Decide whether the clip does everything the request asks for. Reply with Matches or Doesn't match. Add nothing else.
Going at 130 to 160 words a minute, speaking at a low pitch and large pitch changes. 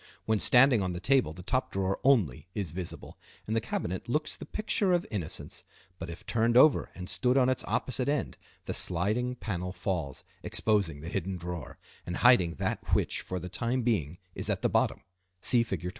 Doesn't match